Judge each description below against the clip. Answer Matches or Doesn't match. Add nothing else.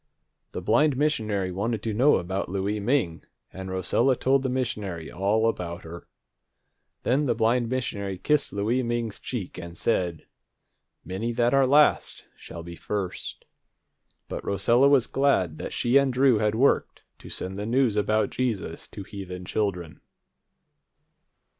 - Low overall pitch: Matches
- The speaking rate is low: Doesn't match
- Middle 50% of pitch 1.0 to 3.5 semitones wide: Doesn't match